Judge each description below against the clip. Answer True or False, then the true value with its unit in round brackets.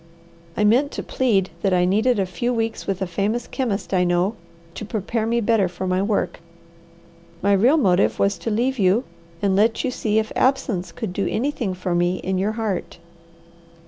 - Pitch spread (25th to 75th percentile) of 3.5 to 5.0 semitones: True (3.8 semitones)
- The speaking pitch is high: True (205 Hz)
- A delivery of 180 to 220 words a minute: True (190 wpm)